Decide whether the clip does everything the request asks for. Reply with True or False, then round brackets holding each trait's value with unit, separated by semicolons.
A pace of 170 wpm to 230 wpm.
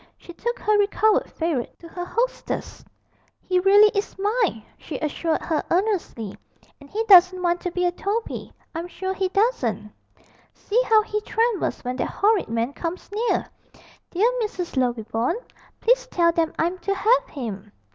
False (160 wpm)